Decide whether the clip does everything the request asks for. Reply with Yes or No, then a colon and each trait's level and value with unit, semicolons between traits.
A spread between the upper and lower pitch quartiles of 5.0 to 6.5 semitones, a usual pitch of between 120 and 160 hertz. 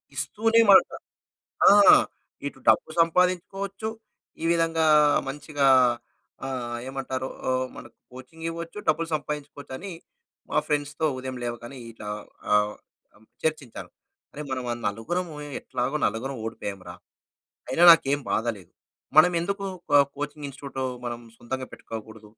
Yes: wide, 5.5 semitones; medium, 140 Hz